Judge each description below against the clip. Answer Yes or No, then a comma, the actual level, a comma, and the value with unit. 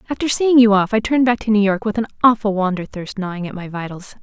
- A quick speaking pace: Yes, fast, 270 wpm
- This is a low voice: No, high, 210 Hz